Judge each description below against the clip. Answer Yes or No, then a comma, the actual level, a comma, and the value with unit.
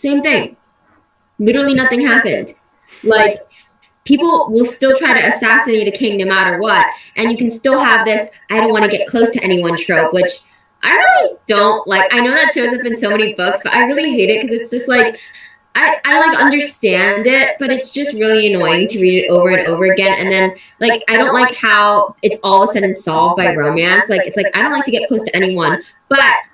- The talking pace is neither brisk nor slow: No, fast, 220 wpm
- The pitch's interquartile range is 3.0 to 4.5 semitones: No, average, 5.2 semitones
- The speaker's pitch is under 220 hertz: No, high, 225 Hz